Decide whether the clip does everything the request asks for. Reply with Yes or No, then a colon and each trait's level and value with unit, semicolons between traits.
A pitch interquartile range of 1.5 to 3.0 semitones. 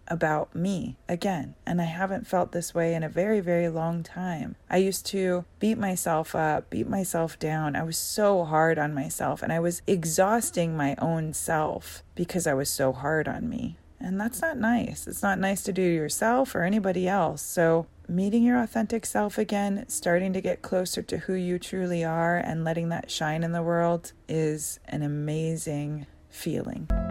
No: average, 3.5 semitones